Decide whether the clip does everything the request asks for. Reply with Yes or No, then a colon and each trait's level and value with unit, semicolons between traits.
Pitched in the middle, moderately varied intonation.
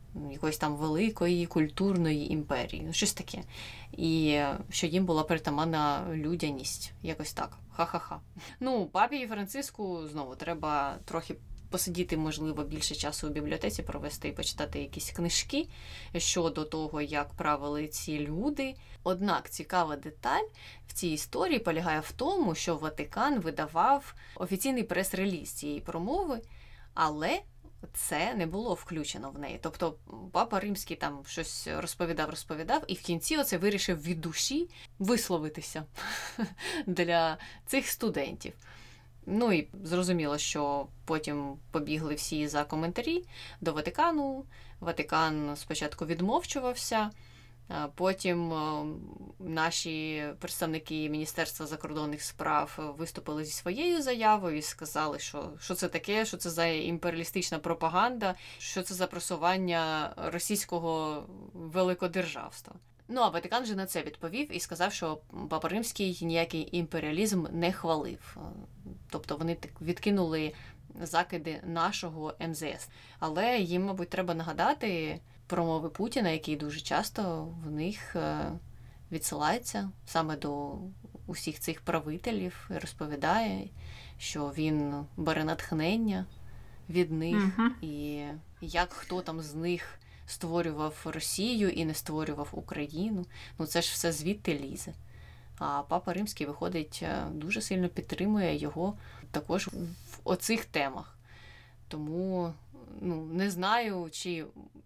Yes: medium, 165 Hz; average, 3.2 semitones